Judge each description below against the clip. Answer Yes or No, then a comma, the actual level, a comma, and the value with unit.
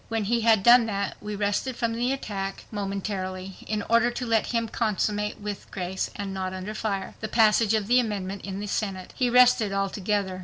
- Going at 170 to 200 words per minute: Yes, average, 195 wpm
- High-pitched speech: Yes, high, 210 Hz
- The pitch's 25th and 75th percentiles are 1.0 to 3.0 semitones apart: Yes, average, 2.7 semitones